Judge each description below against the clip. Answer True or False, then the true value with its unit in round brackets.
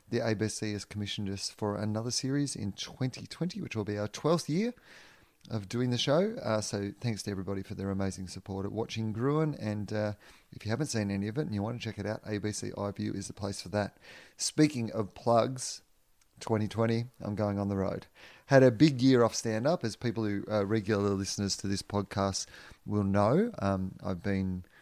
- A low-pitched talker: True (105 Hz)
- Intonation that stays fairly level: False (3.0 semitones)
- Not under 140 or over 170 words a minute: False (205 wpm)